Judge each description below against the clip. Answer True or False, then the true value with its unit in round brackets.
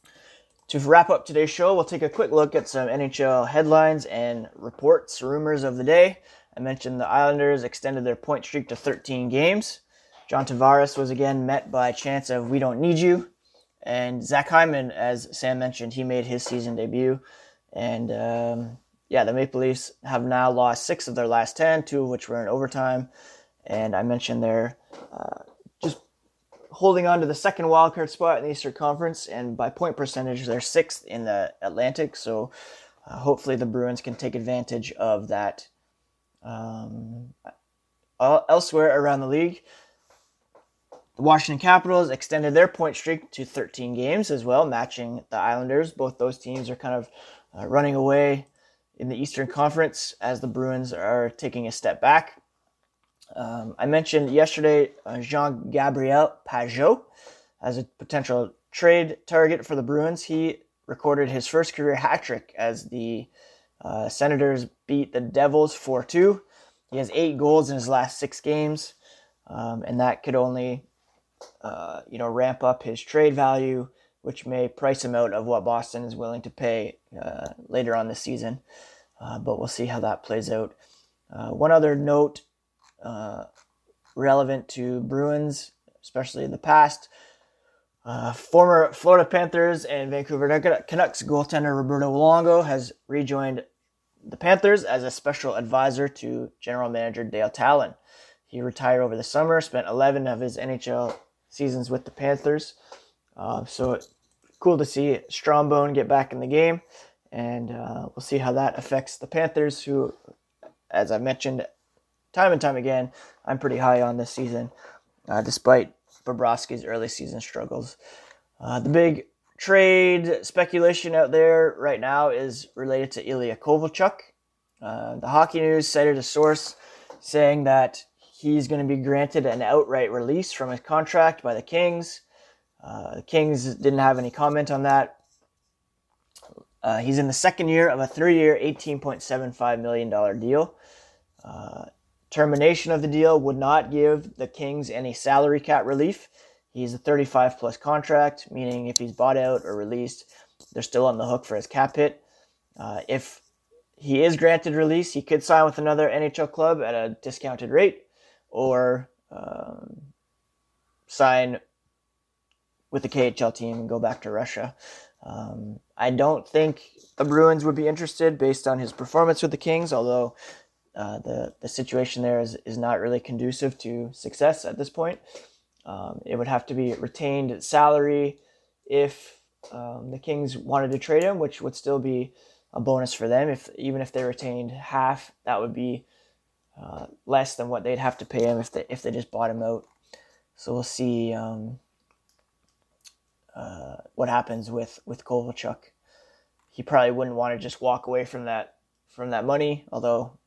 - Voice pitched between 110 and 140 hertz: True (135 Hz)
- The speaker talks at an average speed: True (165 wpm)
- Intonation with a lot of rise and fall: False (3.6 semitones)